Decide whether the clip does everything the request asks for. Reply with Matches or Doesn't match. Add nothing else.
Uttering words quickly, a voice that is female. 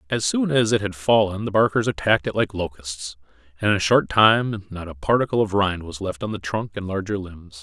Doesn't match